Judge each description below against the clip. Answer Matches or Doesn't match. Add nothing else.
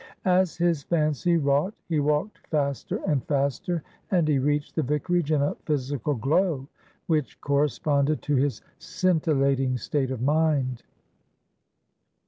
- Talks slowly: Matches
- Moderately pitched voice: Matches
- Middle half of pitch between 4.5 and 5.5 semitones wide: Doesn't match